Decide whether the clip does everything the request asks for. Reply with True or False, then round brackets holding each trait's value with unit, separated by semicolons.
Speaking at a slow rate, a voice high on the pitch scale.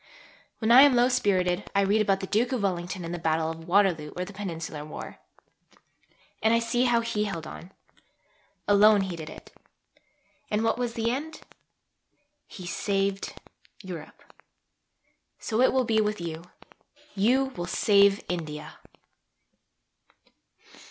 False (145 wpm; 200 Hz)